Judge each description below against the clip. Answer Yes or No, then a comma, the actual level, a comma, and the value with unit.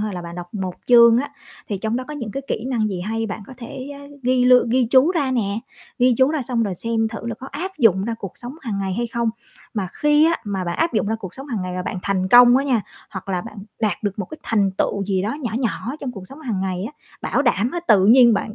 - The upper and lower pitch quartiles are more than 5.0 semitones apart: No, average, 4.5 semitones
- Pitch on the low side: No, high, 230 Hz